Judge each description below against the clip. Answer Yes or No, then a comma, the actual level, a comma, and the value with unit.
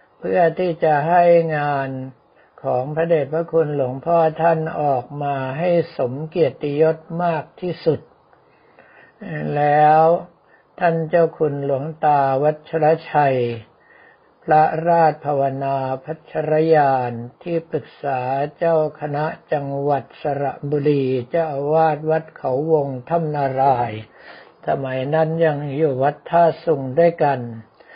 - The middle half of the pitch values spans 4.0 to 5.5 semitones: No, average, 3.0 semitones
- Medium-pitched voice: Yes, medium, 150 Hz